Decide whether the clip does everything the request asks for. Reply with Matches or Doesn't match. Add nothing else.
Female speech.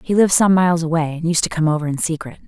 Matches